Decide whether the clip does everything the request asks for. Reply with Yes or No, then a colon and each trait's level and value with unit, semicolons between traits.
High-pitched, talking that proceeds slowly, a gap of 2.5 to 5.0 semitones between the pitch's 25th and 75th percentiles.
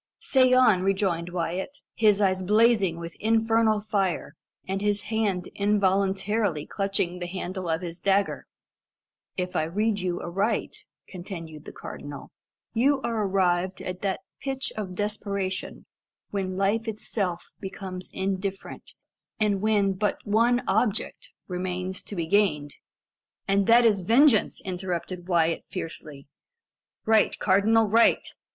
Yes: high, 195 Hz; slow, 130 wpm; average, 2.9 semitones